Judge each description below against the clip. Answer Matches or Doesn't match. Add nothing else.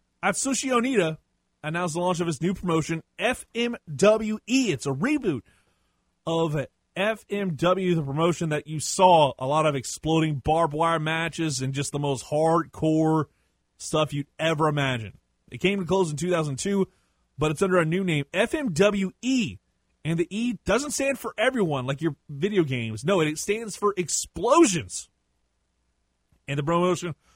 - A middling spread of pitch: Matches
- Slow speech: Doesn't match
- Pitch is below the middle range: Doesn't match